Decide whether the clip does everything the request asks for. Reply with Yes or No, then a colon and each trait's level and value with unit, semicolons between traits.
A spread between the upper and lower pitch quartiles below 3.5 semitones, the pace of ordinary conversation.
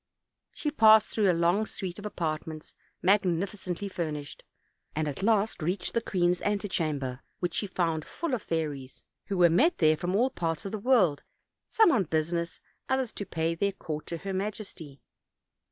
No: average, 4.4 semitones; average, 170 wpm